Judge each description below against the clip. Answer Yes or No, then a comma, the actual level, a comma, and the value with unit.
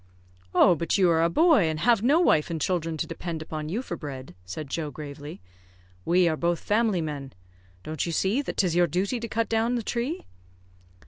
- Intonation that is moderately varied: No, wide, 6.2 semitones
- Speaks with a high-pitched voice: No, medium, 170 Hz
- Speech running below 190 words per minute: No, fast, 205 wpm